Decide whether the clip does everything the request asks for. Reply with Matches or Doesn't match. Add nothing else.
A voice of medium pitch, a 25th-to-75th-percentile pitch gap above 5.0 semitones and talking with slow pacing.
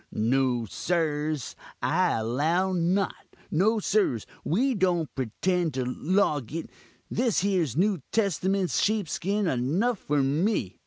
Matches